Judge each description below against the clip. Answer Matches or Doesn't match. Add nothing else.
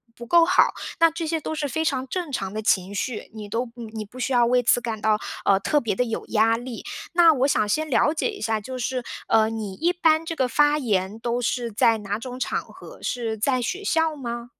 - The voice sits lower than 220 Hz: Doesn't match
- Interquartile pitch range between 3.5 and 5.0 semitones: Doesn't match